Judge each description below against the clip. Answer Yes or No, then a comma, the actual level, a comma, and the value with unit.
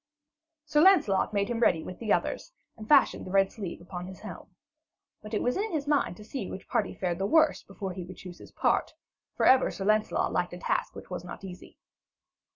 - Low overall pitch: No, high, 195 Hz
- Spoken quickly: Yes, fast, 220 wpm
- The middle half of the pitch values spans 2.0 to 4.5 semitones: No, average, 5.3 semitones